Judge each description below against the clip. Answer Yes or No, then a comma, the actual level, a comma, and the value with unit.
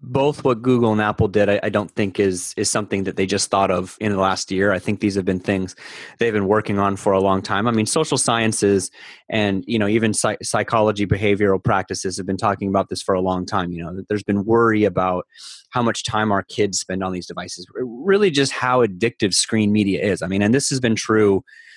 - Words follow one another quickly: Yes, fast, 235 wpm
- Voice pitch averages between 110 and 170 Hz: No, low, 100 Hz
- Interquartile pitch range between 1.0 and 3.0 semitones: Yes, narrow, 2.5 semitones